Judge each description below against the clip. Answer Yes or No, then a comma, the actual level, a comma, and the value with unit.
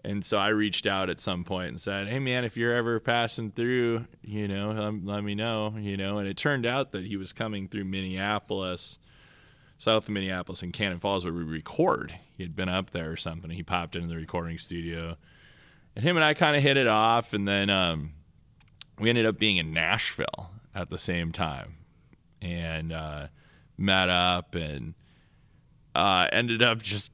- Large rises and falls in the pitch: No, average, 4.3 semitones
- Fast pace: No, average, 190 wpm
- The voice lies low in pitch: Yes, low, 100 Hz